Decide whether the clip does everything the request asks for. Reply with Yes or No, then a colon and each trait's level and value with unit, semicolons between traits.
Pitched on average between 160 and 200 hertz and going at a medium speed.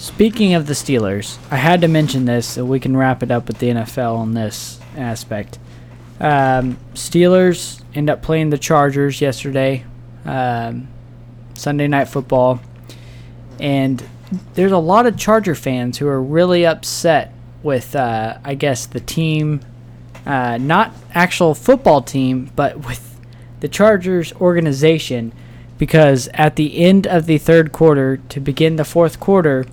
No: low, 135 Hz; average, 145 wpm